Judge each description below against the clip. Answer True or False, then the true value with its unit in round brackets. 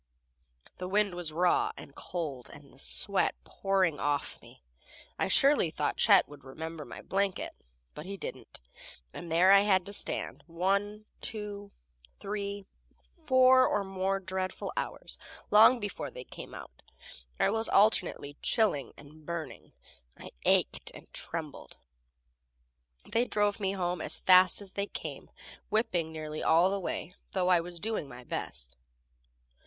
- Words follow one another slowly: False (145 wpm)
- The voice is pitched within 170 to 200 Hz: True (185 Hz)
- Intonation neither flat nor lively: True (4.0 semitones)